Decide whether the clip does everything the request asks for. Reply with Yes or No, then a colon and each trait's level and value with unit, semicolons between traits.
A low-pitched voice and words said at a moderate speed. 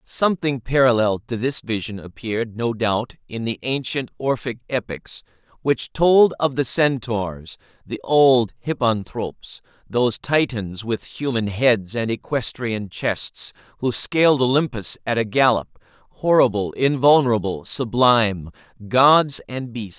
No: low, 120 Hz; slow, 120 wpm